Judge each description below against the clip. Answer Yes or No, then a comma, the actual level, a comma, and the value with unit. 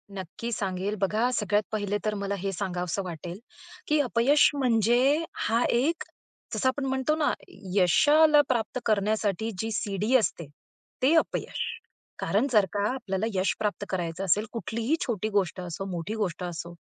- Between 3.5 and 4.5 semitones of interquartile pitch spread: Yes, average, 4.1 semitones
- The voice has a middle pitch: No, high, 210 Hz